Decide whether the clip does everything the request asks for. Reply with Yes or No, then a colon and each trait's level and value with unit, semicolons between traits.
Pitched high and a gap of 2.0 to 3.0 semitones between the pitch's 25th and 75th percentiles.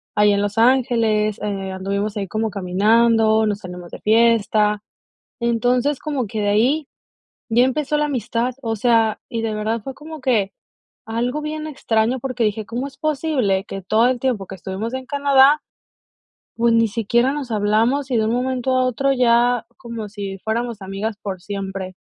No: high, 230 Hz; average, 3.6 semitones